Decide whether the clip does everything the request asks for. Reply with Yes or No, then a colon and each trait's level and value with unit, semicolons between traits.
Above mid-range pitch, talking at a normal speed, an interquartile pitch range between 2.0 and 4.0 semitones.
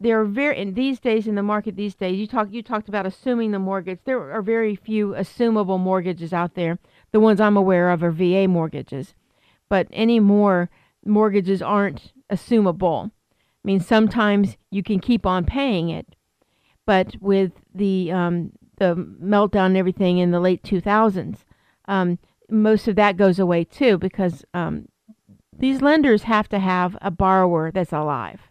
Yes: high, 195 Hz; average, 165 wpm; average, 3.0 semitones